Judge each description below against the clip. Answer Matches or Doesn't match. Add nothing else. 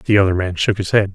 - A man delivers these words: Matches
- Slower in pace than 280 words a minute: Doesn't match